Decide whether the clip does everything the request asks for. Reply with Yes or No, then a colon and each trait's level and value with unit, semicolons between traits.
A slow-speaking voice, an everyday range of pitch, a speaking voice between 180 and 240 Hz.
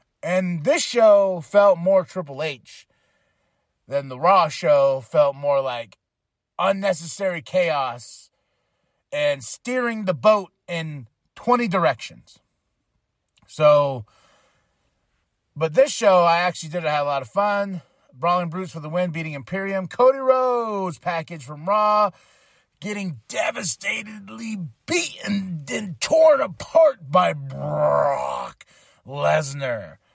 No: slow, 110 wpm; wide, 5.7 semitones; medium, 185 Hz